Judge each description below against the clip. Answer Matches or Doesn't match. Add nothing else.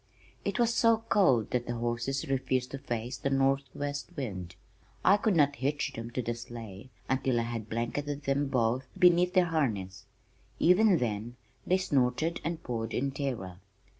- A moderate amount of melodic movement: Matches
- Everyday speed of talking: Matches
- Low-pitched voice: Matches